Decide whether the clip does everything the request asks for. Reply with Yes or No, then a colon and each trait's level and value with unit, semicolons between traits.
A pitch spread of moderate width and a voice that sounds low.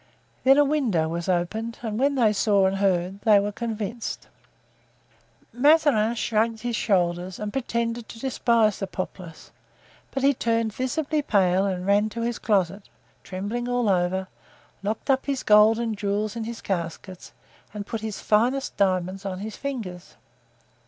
No: average, 3.6 semitones; high, 215 Hz